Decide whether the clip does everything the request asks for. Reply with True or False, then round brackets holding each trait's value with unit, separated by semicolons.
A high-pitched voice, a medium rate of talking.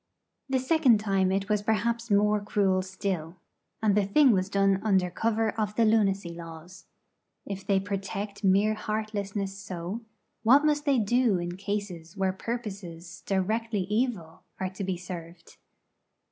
True (200 Hz; 145 wpm)